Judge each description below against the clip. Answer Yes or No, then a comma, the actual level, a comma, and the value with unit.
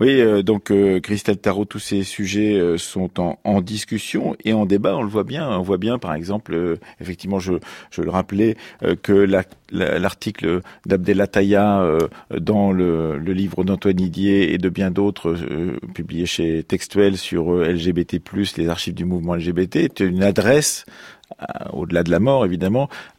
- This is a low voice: Yes, very low, 95 Hz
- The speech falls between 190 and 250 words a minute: No, average, 180 wpm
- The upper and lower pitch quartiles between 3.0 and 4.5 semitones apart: No, narrow, 2.4 semitones